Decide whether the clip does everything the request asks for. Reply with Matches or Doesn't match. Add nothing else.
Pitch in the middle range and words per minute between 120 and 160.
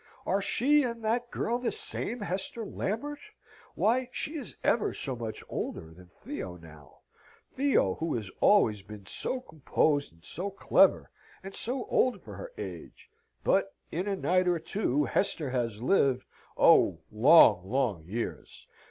Matches